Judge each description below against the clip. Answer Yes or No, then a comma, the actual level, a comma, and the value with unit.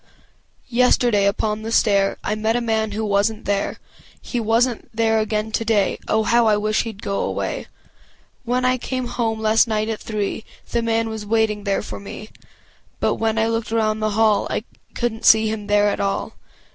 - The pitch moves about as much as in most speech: No, narrow, 1.2 semitones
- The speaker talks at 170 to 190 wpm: Yes, average, 185 wpm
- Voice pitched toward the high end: Yes, high, 220 Hz